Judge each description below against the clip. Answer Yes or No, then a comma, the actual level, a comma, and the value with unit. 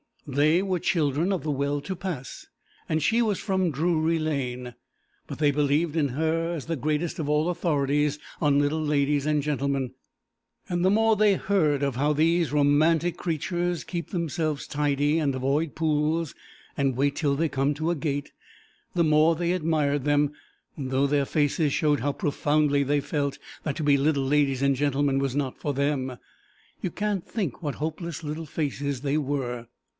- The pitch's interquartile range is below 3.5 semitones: Yes, narrow, 2.6 semitones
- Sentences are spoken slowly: No, average, 175 wpm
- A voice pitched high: No, medium, 150 Hz